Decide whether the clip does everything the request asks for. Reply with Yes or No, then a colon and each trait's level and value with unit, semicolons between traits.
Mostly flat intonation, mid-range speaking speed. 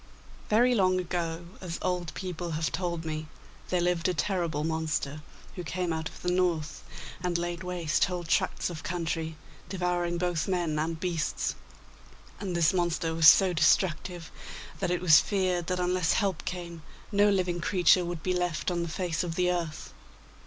Yes: narrow, 1.9 semitones; average, 170 wpm